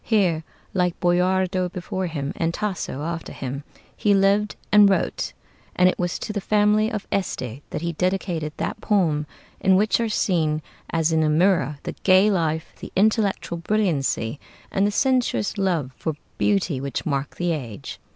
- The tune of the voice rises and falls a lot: No, average, 4.3 semitones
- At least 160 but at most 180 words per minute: Yes, average, 165 wpm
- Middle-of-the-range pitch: Yes, medium, 180 Hz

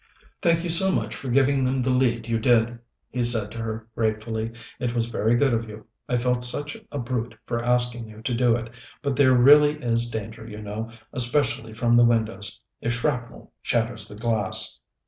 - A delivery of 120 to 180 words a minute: No, average, 195 wpm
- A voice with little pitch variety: Yes, narrow, 2.1 semitones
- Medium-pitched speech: No, low, 120 Hz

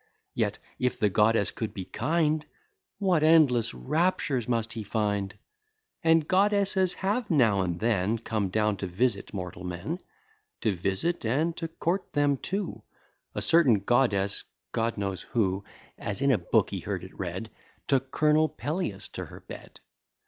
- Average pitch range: No, wide, 8.1 semitones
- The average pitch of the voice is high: No, low, 120 Hz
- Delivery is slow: No, average, 155 wpm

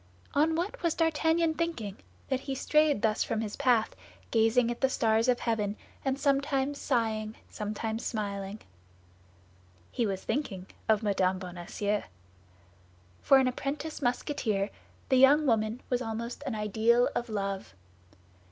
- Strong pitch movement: No, average, 4.5 semitones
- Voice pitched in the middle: No, high, 235 Hz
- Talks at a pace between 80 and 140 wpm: Yes, slow, 135 wpm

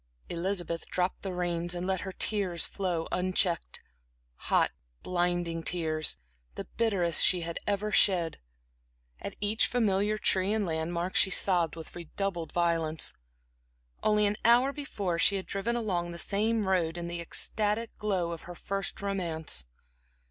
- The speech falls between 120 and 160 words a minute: Yes, average, 145 wpm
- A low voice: No, medium, 180 Hz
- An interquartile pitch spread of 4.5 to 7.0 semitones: No, average, 3.0 semitones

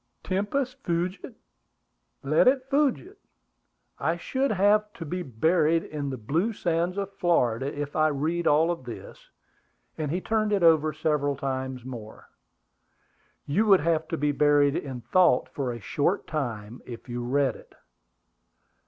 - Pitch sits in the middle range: Yes, medium, 155 Hz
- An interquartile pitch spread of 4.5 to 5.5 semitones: Yes, average, 5.1 semitones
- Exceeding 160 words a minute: No, average, 145 wpm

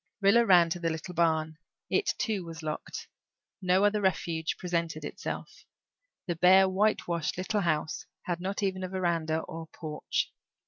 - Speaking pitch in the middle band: Yes, medium, 175 Hz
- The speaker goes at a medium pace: Yes, average, 150 wpm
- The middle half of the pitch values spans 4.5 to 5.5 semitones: No, average, 2.8 semitones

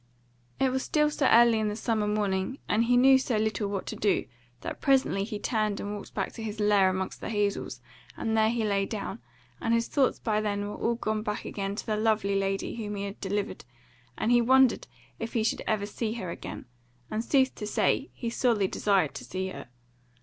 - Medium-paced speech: No, fast, 215 wpm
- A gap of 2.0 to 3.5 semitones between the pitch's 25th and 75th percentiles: Yes, narrow, 2.4 semitones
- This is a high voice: Yes, high, 215 Hz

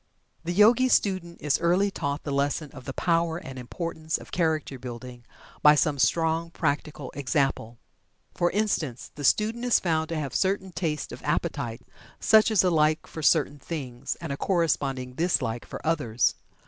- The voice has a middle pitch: Yes, medium, 155 Hz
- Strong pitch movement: No, average, 4.2 semitones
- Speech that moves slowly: No, average, 165 wpm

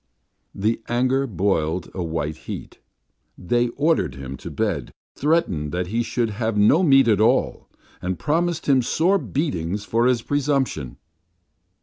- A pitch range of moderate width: No, wide, 7.3 semitones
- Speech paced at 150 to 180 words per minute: No, average, 140 wpm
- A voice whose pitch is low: Yes, low, 115 Hz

